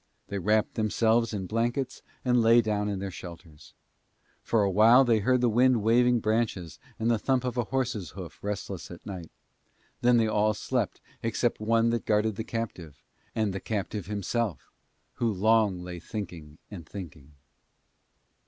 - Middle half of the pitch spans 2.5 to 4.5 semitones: Yes, average, 3.3 semitones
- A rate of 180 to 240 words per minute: No, average, 160 wpm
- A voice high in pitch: No, low, 110 Hz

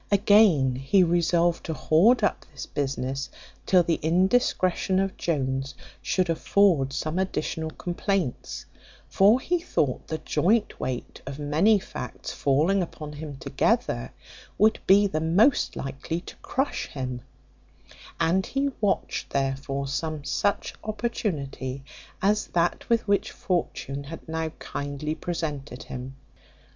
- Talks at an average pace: No, slow, 125 wpm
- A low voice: No, medium, 160 Hz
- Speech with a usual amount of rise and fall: No, wide, 5.9 semitones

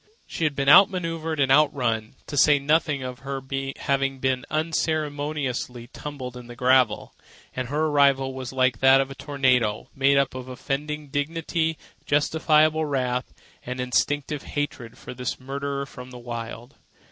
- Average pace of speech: Yes, average, 155 wpm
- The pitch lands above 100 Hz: Yes, low, 135 Hz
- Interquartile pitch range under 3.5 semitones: Yes, average, 2.8 semitones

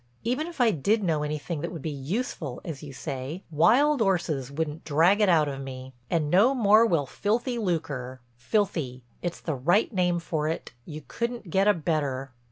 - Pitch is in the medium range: Yes, medium, 165 Hz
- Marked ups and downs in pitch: Yes, wide, 6.3 semitones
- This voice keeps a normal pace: Yes, average, 180 wpm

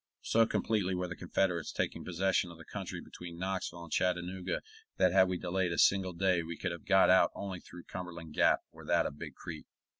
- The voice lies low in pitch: Yes, very low, 90 Hz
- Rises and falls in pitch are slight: Yes, narrow, 1.7 semitones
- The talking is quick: Yes, fast, 210 wpm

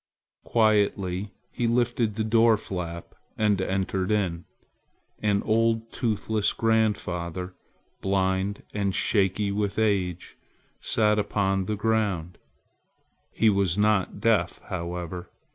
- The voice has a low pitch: Yes, low, 100 Hz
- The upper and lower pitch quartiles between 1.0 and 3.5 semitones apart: Yes, narrow, 2.6 semitones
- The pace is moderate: No, slow, 105 wpm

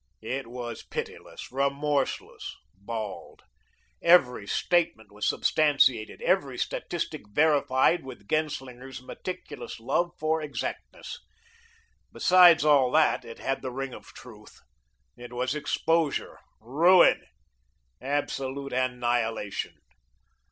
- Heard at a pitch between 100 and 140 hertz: Yes, low, 135 Hz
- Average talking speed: No, slow, 95 wpm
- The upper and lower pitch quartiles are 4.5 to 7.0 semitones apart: No, average, 3.9 semitones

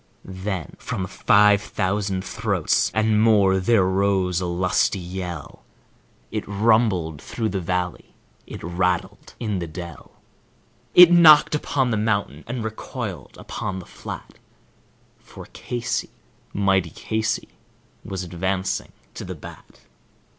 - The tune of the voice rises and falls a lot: No, average, 3.1 semitones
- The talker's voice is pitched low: Yes, very low, 95 Hz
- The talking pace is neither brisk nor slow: No, slow, 120 wpm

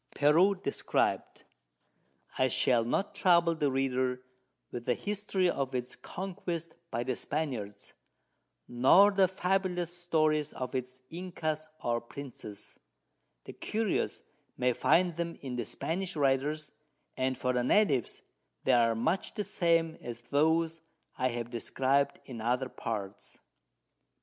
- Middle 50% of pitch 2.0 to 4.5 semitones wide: No, wide, 5.4 semitones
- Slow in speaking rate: Yes, slow, 130 wpm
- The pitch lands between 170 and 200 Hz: No, medium, 140 Hz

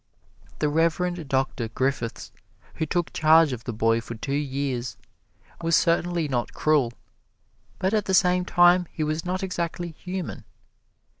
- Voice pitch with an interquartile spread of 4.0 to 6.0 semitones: Yes, average, 4.7 semitones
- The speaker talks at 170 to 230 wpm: No, average, 145 wpm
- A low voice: No, medium, 160 Hz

